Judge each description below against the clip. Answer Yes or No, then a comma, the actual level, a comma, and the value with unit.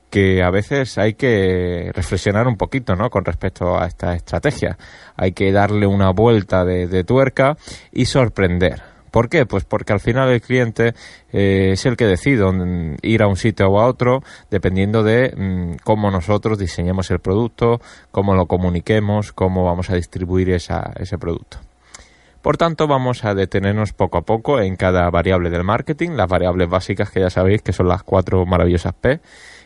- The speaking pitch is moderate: No, very low, 95 Hz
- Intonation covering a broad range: No, average, 3.8 semitones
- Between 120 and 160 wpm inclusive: No, average, 175 wpm